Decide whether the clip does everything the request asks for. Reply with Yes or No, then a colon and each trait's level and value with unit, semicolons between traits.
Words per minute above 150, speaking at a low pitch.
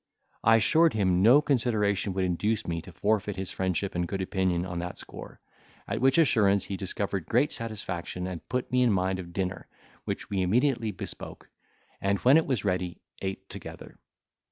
Yes: average, 180 wpm; low, 100 Hz